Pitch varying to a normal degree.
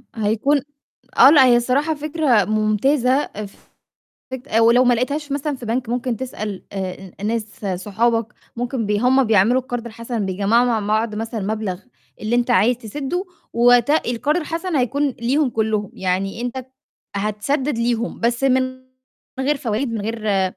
Yes: average, 3.6 semitones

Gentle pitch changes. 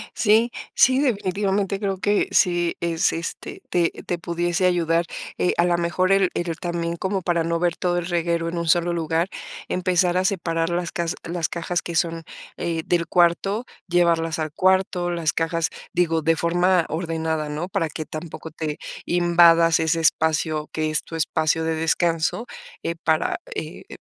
Yes: narrow, 1.4 semitones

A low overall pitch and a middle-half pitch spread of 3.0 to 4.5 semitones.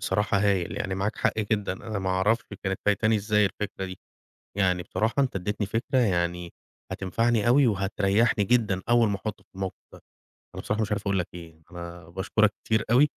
No: low, 100 Hz; narrow, 2.6 semitones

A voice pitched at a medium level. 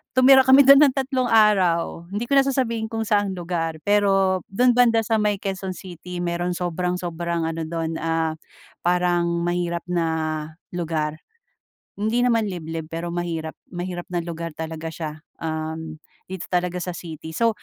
Yes: medium, 175 Hz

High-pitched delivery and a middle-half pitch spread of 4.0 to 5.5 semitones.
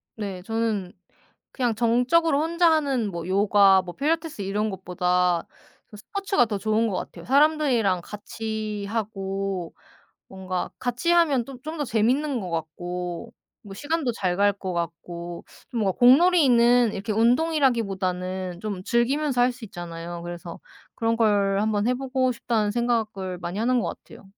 Yes: high, 215 Hz; average, 5.1 semitones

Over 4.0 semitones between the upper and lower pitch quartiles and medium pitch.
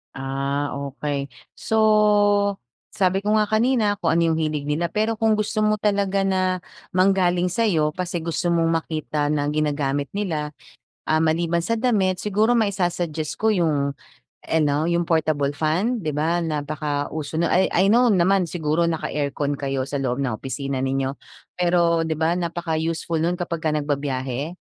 Yes: average, 4.6 semitones; medium, 165 Hz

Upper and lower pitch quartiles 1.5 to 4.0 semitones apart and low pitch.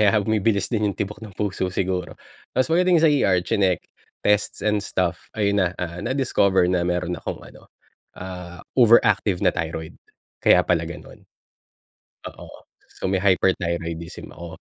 Yes: average, 3.1 semitones; very low, 95 Hz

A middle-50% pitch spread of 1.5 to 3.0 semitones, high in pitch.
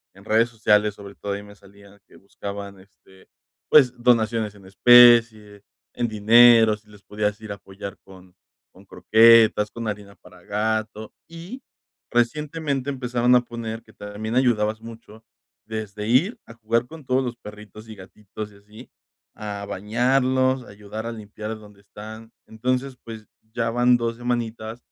No: narrow, 2.6 semitones; low, 110 Hz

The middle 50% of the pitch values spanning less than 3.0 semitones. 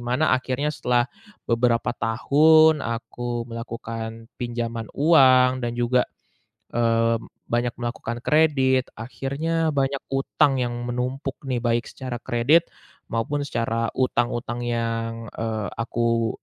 Yes: narrow, 2.5 semitones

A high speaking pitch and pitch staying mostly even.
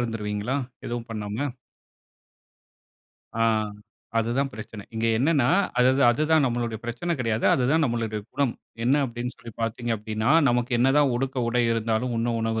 No: low, 120 Hz; narrow, 2.2 semitones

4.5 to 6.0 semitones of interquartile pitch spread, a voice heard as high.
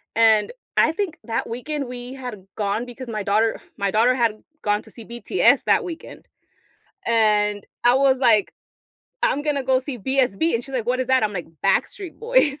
No: average, 4.0 semitones; high, 245 Hz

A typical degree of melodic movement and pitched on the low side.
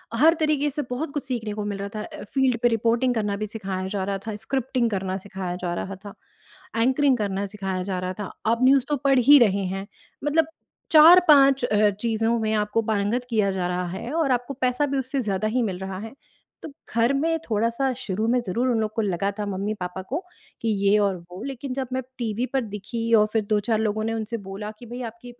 No: average, 4.2 semitones; high, 225 Hz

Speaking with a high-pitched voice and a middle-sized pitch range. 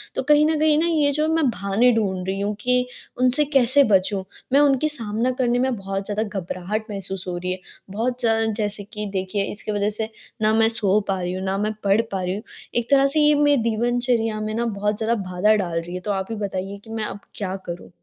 Yes: high, 215 Hz; average, 4.1 semitones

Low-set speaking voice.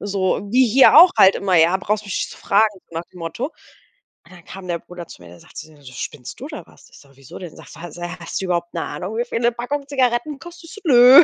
No: high, 195 Hz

